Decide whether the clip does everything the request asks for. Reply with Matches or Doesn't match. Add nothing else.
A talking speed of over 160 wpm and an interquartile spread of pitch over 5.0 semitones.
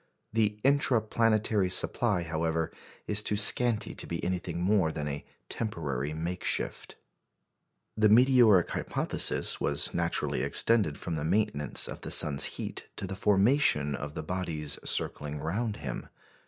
Doesn't match